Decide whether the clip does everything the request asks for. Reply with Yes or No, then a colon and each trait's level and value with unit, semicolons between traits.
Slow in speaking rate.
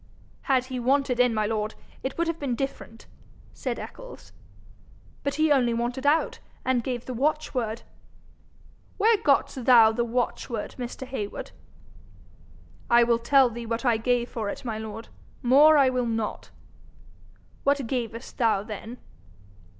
No: average, 145 wpm